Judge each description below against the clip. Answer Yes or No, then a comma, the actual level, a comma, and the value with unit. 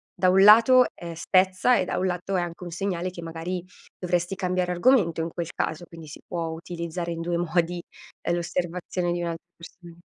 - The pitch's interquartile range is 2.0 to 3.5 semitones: No, narrow, 1.5 semitones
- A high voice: No, medium, 175 Hz